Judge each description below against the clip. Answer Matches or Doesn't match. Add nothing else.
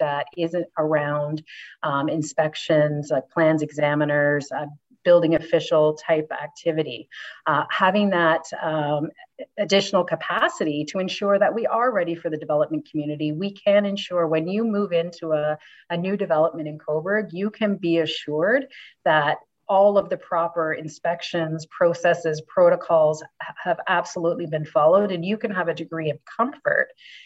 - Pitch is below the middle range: Doesn't match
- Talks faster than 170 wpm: Doesn't match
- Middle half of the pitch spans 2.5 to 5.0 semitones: Matches